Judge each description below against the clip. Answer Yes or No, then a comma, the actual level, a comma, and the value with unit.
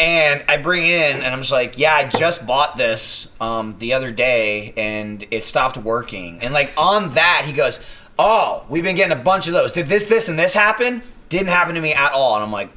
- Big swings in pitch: Yes, wide, 7.5 semitones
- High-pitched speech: No, medium, 140 Hz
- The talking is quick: Yes, fast, 240 wpm